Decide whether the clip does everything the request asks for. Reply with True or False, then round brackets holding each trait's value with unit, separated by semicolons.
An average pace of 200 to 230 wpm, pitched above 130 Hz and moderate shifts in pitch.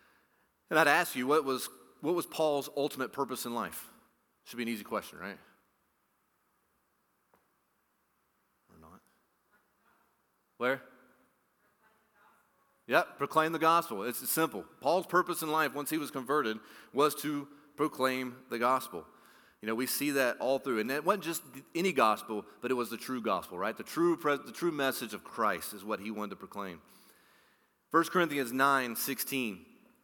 False (155 wpm; 140 Hz; 4.4 semitones)